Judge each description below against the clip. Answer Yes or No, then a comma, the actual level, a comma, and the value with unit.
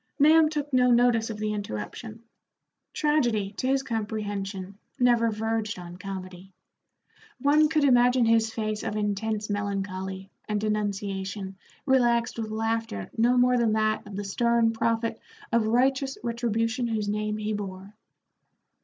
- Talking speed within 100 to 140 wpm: Yes, slow, 135 wpm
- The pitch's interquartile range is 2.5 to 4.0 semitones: Yes, average, 2.8 semitones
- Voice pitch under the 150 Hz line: No, high, 220 Hz